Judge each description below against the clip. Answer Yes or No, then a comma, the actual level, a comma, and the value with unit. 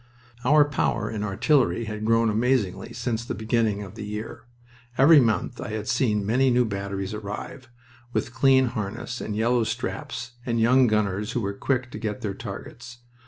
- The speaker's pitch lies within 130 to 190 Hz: No, low, 115 Hz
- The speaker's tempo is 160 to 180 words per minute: Yes, average, 170 wpm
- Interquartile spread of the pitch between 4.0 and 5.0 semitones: No, average, 2.7 semitones